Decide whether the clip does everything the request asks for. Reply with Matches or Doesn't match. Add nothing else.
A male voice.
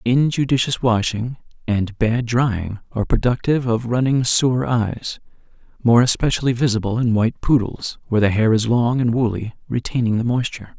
Matches